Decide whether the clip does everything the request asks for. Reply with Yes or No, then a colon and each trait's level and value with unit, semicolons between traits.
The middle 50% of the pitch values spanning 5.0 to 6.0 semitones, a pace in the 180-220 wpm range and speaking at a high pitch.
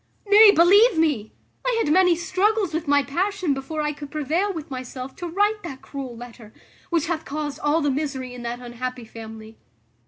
Yes: wide, 5.6 semitones; average, 185 wpm; very high, 300 Hz